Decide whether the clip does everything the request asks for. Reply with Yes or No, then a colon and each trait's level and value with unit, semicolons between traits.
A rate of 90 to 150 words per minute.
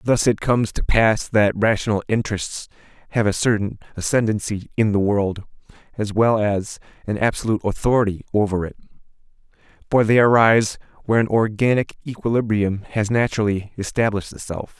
Yes: average, 140 wpm